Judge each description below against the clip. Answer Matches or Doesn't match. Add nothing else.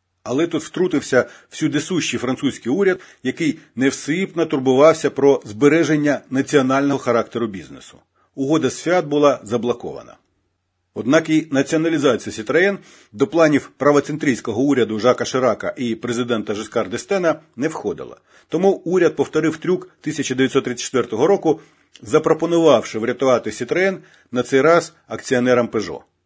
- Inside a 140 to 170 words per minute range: Doesn't match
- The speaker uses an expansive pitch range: Doesn't match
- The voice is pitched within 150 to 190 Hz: Doesn't match